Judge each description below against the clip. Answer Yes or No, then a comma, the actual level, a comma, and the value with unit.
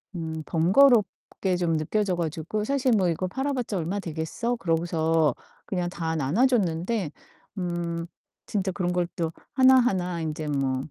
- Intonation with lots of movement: No, average, 4.4 semitones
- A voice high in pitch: No, medium, 175 Hz